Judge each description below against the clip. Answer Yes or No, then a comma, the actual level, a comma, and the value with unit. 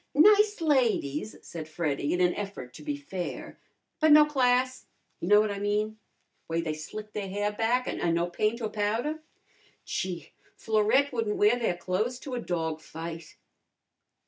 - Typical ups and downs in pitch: No, wide, 6.2 semitones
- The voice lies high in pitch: Yes, high, 210 Hz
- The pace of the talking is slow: No, average, 165 wpm